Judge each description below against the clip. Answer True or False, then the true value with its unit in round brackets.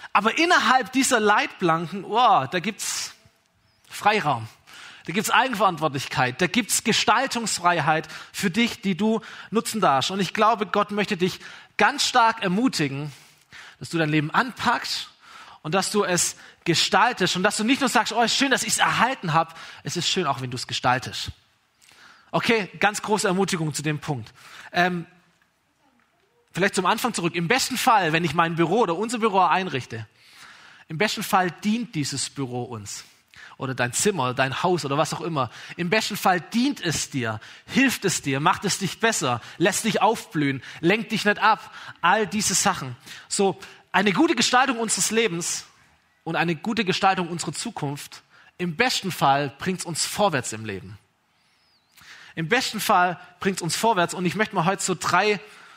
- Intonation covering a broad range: True (5.7 semitones)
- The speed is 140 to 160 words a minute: False (170 wpm)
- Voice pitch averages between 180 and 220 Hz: True (185 Hz)